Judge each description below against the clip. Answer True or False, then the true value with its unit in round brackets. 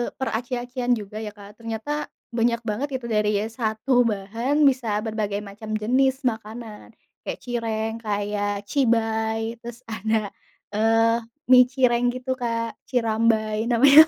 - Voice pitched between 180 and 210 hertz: False (225 Hz)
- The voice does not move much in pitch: True (2.2 semitones)